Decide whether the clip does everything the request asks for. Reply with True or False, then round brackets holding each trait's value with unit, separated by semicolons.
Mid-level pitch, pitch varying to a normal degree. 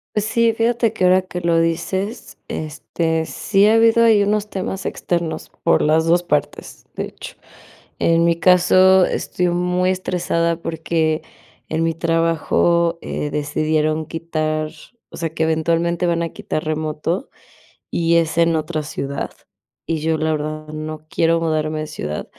False (165 Hz; 2.3 semitones)